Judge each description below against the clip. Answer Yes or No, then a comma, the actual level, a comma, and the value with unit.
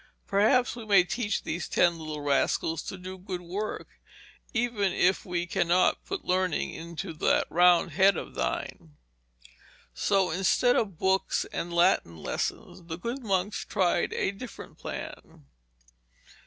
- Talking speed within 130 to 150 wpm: Yes, average, 140 wpm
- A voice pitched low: No, medium, 185 Hz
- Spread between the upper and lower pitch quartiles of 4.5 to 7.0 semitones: No, average, 2.8 semitones